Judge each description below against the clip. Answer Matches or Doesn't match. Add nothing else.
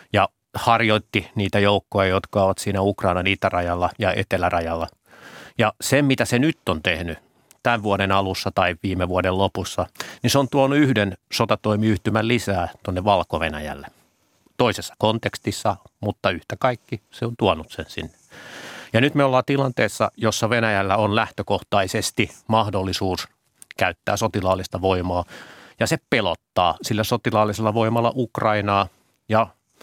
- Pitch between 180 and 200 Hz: Doesn't match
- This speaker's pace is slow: Doesn't match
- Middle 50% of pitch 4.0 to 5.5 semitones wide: Doesn't match